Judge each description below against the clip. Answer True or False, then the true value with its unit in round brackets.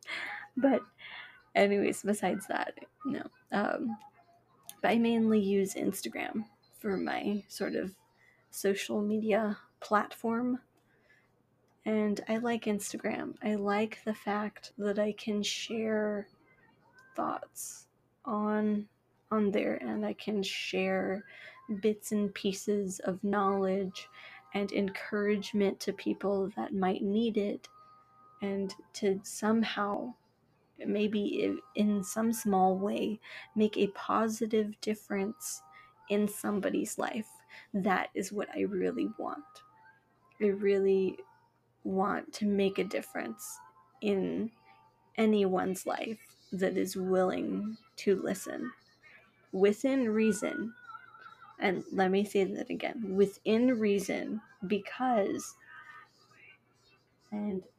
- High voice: True (205 Hz)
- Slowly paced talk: True (105 wpm)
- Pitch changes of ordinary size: False (2.2 semitones)